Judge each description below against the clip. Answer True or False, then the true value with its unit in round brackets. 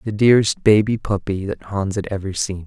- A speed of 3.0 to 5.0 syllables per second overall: False (5.5 syllables/s)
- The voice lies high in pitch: False (100 Hz)